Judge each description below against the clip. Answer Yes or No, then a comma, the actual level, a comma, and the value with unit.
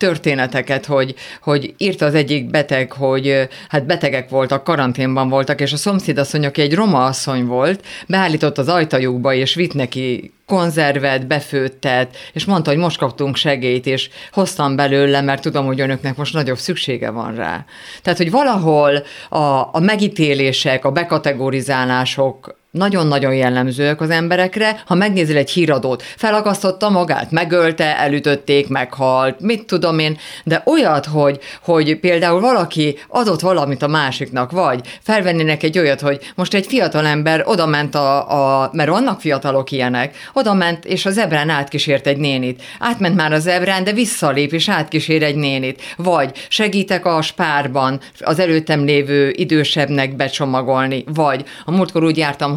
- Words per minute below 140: No, average, 150 wpm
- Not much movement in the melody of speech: No, average, 4.3 semitones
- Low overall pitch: No, medium, 150 Hz